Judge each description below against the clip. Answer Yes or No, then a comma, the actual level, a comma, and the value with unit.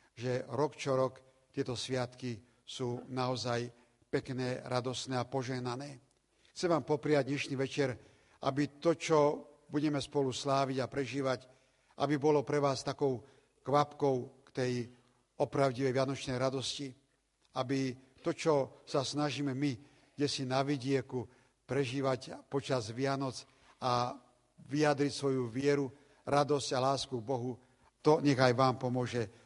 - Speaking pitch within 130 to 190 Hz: Yes, low, 135 Hz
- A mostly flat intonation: Yes, narrow, 2.0 semitones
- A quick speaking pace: No, average, 125 wpm